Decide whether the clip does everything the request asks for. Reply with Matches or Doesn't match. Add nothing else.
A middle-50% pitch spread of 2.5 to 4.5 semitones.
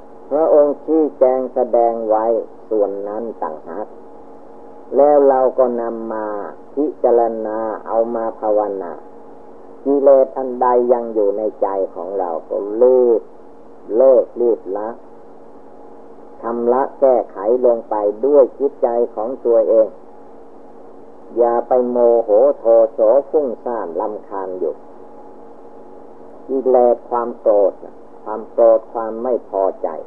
Doesn't match